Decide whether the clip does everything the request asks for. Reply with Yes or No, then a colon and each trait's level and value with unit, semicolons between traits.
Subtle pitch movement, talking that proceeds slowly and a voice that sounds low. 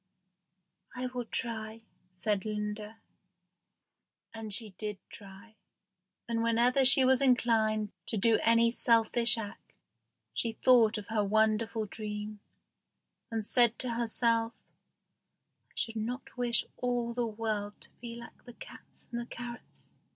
No: narrow, 1.9 semitones; slow, 130 wpm; high, 225 Hz